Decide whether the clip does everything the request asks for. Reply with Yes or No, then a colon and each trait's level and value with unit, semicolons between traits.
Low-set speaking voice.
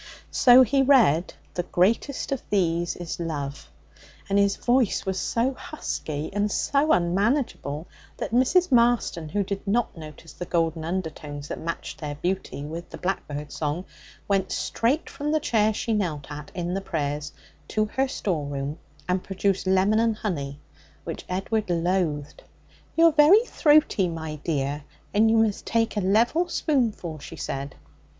No: high, 190 Hz